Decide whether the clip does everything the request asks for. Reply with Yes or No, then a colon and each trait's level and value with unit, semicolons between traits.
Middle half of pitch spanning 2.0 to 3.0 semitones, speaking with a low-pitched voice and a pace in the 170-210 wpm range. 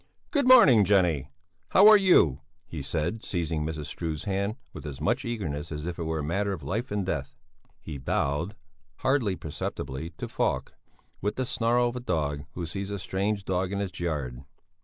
No: wide, 5.4 semitones; very low, 90 Hz; average, 185 wpm